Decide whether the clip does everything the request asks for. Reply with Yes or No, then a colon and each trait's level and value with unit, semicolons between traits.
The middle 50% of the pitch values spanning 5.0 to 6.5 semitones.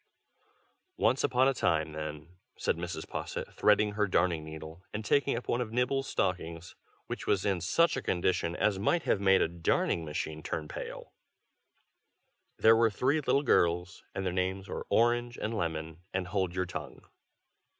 Yes: wide, 5.4 semitones